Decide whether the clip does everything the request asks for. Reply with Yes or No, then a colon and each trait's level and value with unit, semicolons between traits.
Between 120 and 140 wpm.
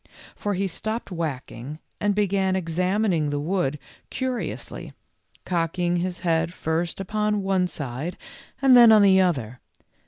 Yes: slow, 135 wpm